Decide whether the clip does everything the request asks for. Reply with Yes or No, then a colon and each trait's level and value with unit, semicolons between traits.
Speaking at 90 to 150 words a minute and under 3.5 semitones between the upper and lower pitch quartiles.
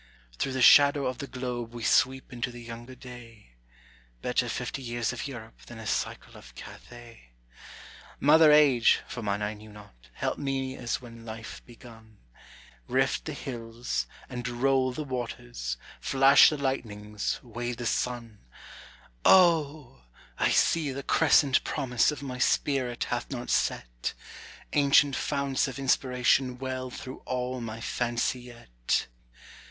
Yes: average, 140 wpm; narrow, 2.6 semitones